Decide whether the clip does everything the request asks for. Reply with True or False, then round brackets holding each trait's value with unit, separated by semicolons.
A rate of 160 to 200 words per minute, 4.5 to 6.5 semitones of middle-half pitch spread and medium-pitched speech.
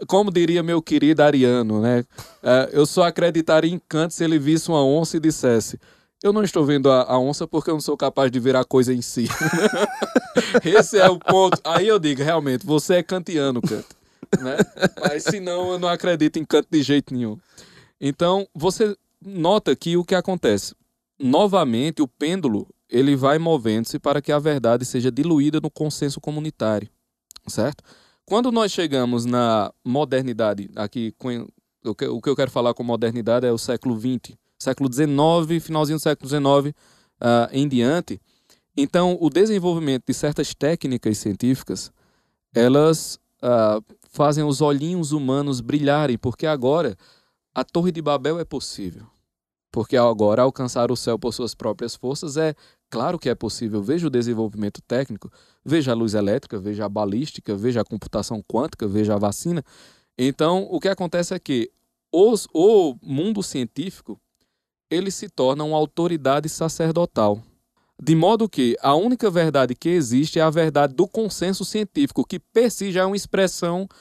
True (165 wpm; 5.6 semitones; 150 Hz)